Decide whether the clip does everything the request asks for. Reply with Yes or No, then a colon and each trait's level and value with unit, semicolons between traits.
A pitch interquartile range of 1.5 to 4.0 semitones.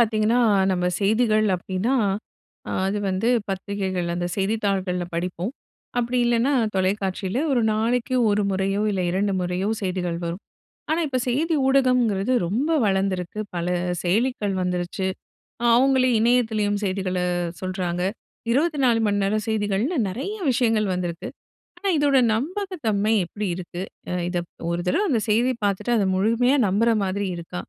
No: average, 4.4 semitones